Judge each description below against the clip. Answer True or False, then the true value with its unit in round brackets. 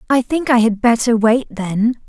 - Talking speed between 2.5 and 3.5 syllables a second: False (4.6 syllables/s)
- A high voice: True (235 Hz)